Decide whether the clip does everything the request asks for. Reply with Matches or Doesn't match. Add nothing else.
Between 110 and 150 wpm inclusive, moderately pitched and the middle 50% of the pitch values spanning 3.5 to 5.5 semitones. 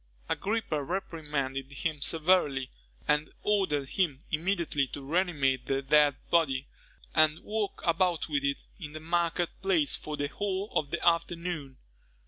Matches